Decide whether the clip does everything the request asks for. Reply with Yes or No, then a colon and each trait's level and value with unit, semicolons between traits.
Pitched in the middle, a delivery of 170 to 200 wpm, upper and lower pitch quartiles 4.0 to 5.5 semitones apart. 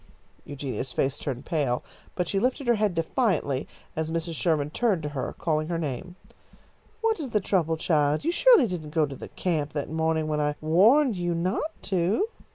Yes: medium, 165 Hz; average, 185 wpm; average, 5.2 semitones